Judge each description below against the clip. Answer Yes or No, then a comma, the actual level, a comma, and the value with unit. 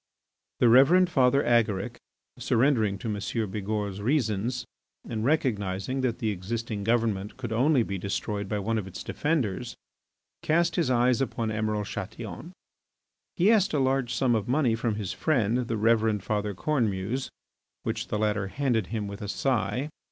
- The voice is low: Yes, low, 115 Hz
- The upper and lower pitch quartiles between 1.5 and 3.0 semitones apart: No, average, 4.0 semitones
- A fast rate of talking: No, average, 155 wpm